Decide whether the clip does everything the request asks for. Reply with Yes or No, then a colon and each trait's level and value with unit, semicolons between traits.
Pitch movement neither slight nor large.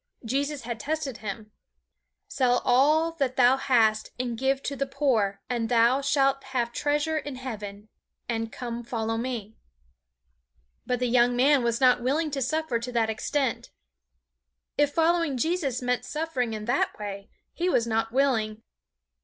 Yes: average, 3.5 semitones